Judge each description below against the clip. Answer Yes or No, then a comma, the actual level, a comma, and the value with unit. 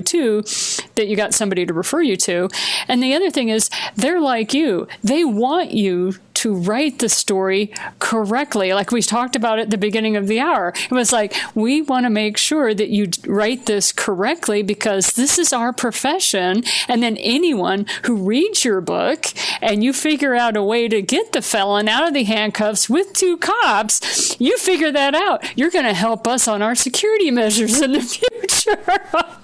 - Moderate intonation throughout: No, wide, 5.9 semitones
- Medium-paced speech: Yes, average, 190 wpm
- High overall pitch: Yes, high, 230 Hz